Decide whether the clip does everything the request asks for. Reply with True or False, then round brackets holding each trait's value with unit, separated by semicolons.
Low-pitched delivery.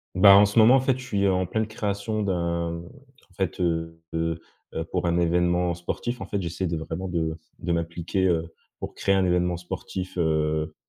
True (90 Hz)